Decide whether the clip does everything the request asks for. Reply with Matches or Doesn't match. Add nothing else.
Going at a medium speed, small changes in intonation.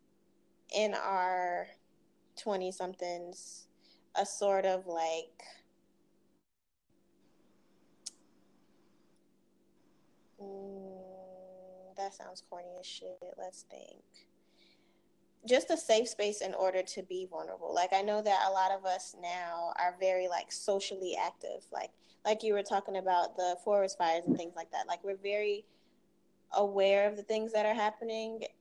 Doesn't match